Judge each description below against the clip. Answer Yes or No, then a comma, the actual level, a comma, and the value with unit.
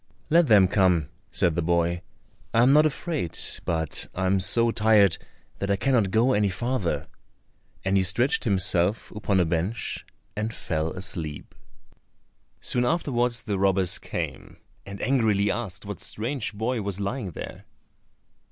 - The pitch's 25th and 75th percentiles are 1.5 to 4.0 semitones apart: No, average, 4.5 semitones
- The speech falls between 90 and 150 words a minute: Yes, average, 145 wpm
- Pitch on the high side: No, low, 100 Hz